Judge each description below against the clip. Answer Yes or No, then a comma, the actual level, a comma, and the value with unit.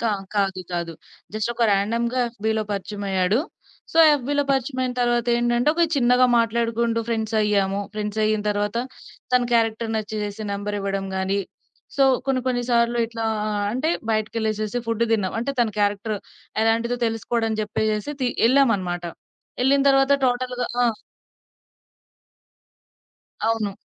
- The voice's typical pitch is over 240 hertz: No, high, 225 Hz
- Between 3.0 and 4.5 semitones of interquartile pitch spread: No, narrow, 2.5 semitones